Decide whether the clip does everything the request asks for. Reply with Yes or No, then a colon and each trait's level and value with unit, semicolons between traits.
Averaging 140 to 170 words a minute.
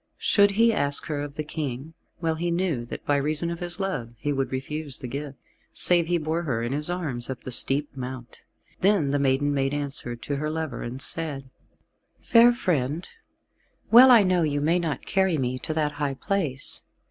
No: average, 195 wpm